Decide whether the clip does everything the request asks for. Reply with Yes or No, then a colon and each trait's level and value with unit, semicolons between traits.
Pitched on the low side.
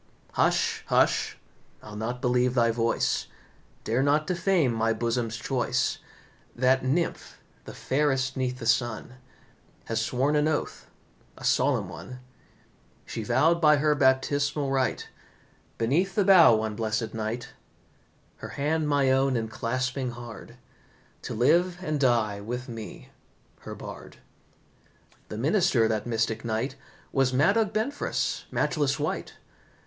Yes: low, 130 Hz